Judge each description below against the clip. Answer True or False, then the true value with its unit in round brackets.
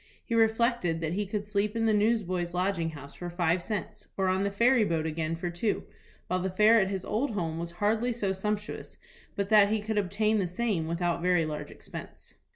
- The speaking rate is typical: False (210 wpm)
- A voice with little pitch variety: False (3.7 semitones)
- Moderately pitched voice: False (195 Hz)